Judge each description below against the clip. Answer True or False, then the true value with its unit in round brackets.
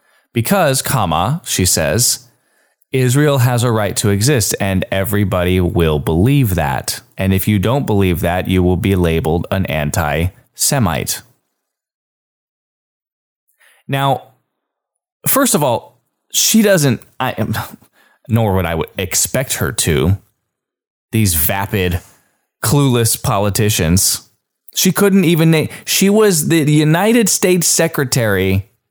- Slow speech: True (115 wpm)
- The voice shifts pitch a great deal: True (7.1 semitones)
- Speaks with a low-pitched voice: True (110 Hz)